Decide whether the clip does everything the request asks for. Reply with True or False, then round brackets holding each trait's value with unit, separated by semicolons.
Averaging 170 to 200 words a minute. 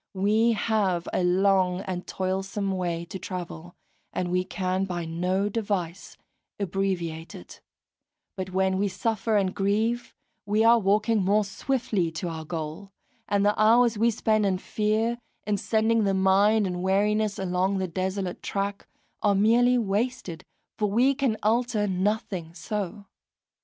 False (145 wpm)